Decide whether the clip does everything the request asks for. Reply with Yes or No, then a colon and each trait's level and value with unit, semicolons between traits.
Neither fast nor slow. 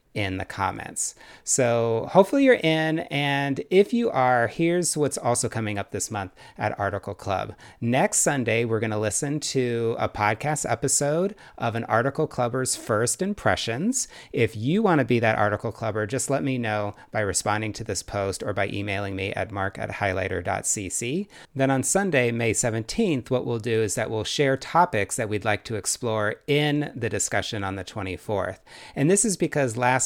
Yes: average, 180 wpm